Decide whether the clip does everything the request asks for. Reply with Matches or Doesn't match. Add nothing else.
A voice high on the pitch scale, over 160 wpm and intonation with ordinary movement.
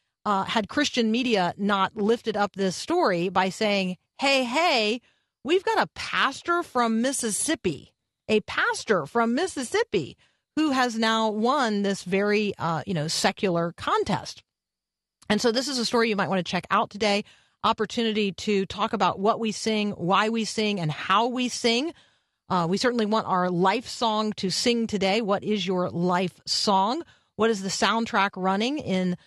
Matches